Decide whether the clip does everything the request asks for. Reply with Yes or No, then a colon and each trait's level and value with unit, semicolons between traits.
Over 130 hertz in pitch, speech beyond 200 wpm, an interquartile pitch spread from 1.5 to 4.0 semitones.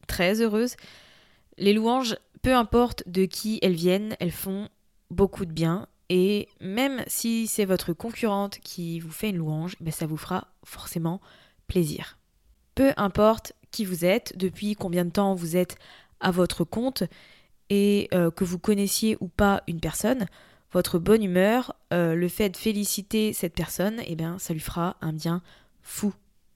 No: high, 190 Hz; average, 165 wpm; average, 3.5 semitones